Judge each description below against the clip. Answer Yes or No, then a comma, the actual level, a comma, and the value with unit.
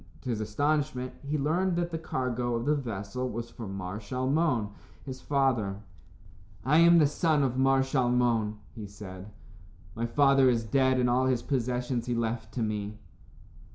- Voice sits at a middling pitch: No, low, 125 Hz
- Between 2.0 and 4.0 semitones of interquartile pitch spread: Yes, average, 3.5 semitones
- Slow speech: No, average, 165 wpm